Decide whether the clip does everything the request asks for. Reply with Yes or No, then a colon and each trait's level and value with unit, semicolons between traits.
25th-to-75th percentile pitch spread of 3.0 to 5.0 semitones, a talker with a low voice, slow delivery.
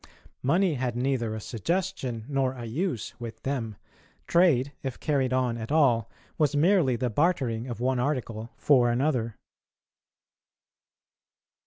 Yes: average, 3.9 semitones; low, 130 Hz; slow, 130 wpm